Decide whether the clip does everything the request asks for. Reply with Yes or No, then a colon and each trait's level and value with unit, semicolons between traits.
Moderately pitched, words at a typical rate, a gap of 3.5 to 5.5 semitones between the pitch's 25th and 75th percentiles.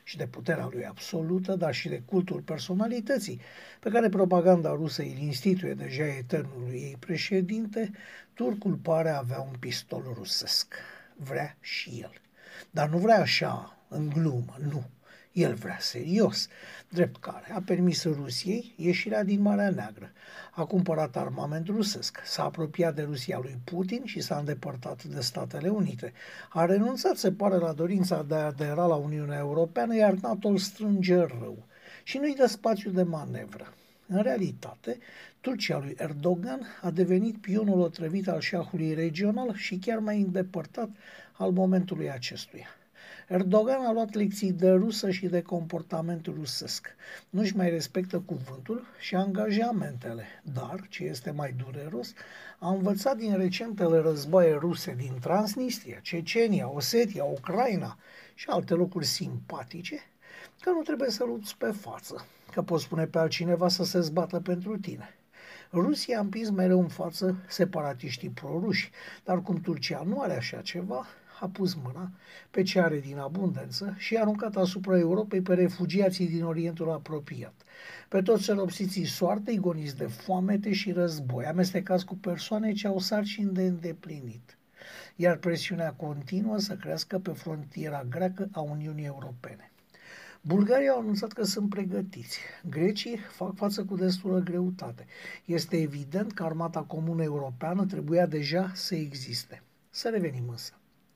Yes: medium, 180 Hz; average, 145 wpm; average, 3.8 semitones